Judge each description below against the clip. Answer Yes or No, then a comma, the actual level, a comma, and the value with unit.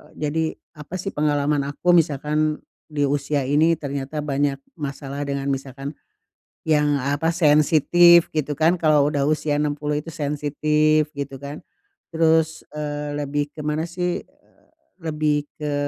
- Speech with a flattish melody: Yes, narrow, 1.5 semitones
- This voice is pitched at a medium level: Yes, medium, 150 Hz